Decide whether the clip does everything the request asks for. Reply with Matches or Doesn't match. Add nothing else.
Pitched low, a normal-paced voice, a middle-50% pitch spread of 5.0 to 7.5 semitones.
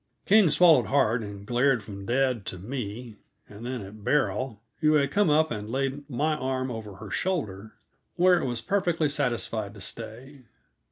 Matches